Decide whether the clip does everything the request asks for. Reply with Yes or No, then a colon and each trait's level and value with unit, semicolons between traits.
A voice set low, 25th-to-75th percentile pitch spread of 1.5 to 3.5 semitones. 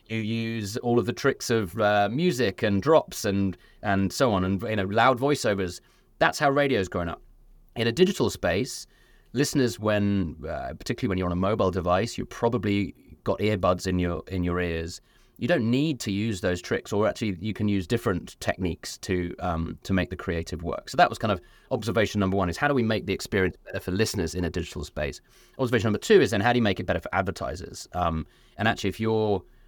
No: low, 100 Hz; average, 4.2 semitones